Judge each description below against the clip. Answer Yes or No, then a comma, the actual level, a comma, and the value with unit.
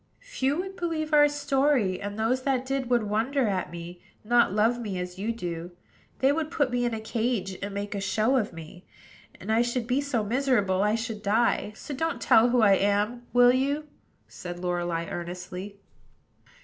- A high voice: Yes, high, 225 Hz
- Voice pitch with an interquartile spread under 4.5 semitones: No, average, 5.1 semitones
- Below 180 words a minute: No, average, 190 wpm